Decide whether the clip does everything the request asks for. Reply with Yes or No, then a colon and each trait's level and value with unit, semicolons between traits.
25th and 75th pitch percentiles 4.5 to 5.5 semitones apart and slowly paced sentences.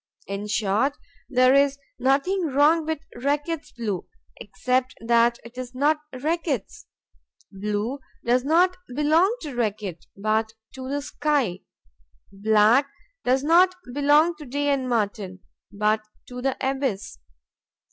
Yes: average, 5.1 semitones; slow, 125 wpm